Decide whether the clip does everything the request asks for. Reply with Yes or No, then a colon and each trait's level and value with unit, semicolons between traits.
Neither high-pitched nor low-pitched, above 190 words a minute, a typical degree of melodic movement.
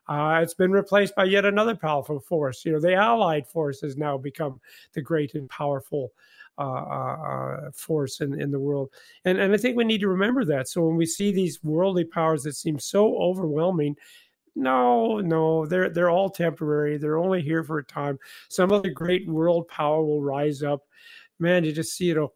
Yes: medium, 160 Hz; average, 200 wpm; average, 3.9 semitones